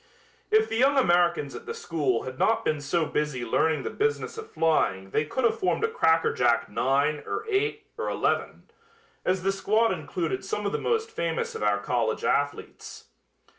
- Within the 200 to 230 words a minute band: No, average, 185 wpm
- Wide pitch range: Yes, wide, 8.4 semitones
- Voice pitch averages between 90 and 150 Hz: No, medium, 165 Hz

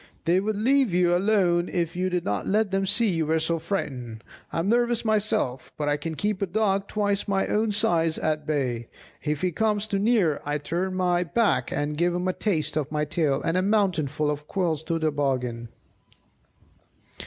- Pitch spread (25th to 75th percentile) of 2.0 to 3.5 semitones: No, average, 5.0 semitones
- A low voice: No, medium, 175 Hz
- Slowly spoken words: No, average, 200 wpm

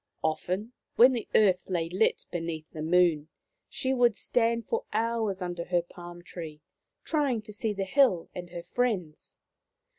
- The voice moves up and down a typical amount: Yes, average, 5.0 semitones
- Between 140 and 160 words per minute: Yes, average, 155 wpm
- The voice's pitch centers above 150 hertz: Yes, medium, 185 Hz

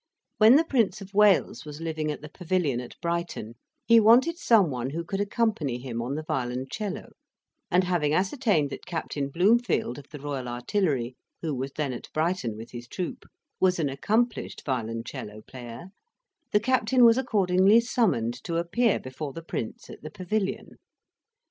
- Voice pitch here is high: No, medium, 165 Hz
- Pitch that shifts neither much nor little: No, wide, 7.9 semitones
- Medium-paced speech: Yes, average, 165 wpm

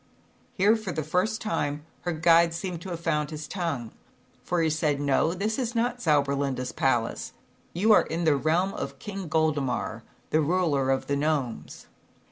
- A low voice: No, medium, 160 Hz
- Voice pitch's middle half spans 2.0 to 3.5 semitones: No, average, 4.3 semitones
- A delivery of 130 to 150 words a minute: No, average, 170 wpm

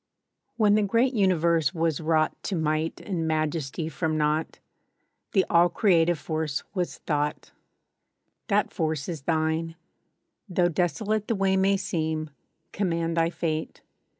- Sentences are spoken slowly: Yes, slow, 130 wpm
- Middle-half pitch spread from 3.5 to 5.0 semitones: No, average, 2.9 semitones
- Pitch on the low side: No, medium, 165 Hz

